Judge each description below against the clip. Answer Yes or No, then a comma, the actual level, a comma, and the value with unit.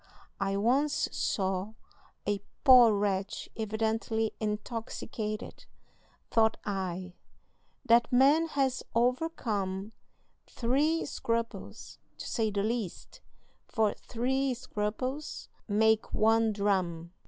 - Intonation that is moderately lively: Yes, average, 3.5 semitones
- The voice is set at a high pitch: Yes, high, 220 Hz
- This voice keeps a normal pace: No, slow, 90 wpm